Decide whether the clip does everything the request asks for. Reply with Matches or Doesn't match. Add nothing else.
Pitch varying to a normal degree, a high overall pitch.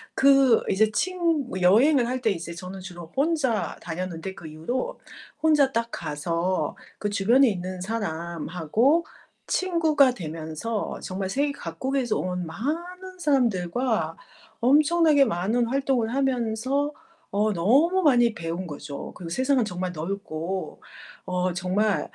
Doesn't match